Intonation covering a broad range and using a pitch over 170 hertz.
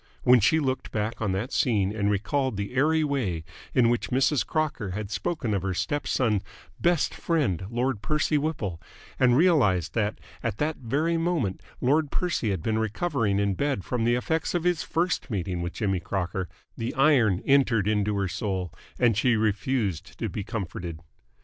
No: wide, 6.1 semitones; low, 115 Hz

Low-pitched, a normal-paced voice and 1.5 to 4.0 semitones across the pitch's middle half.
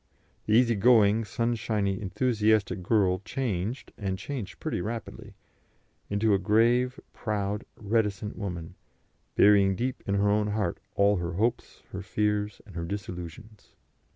No: low, 105 Hz; slow, 130 wpm; narrow, 2.4 semitones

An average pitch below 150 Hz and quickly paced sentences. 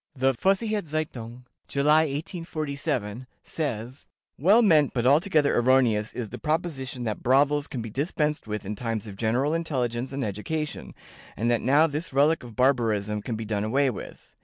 No: low, 135 Hz; average, 160 wpm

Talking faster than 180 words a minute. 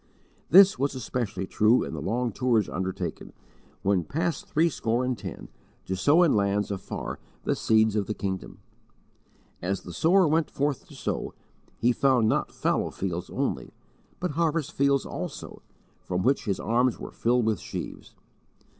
No: average, 155 wpm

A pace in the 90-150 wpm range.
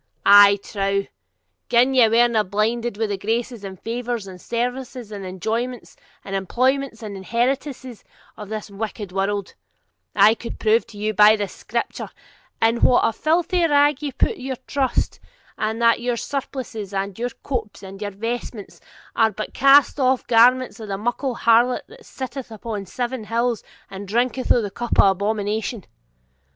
No: average, 160 wpm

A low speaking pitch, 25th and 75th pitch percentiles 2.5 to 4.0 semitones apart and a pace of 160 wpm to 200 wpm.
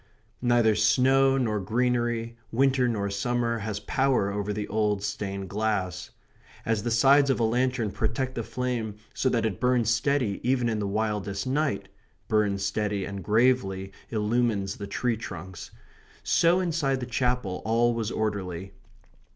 No: low, 115 Hz; average, 3.6 semitones; average, 150 wpm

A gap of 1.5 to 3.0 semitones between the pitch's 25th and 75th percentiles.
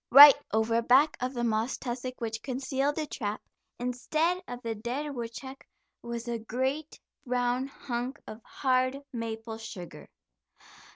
Yes: average, 2.7 semitones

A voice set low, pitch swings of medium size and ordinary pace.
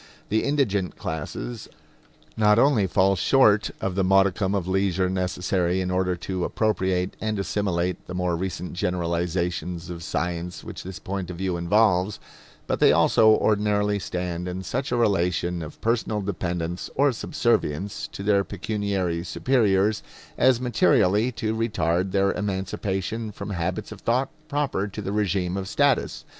Yes: very low, 95 Hz; average, 3.0 semitones; average, 150 wpm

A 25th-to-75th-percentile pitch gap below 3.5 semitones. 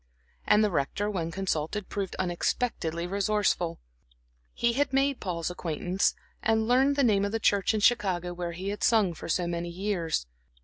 No: average, 3.9 semitones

